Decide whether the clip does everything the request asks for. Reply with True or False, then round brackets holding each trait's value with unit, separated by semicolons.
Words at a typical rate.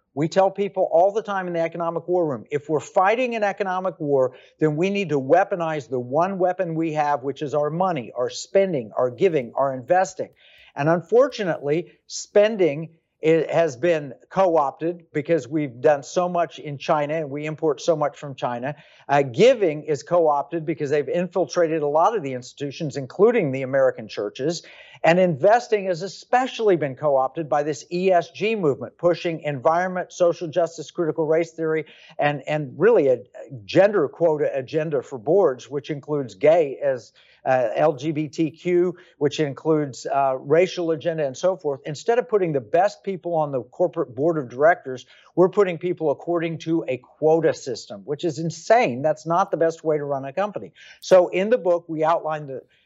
True (175 wpm)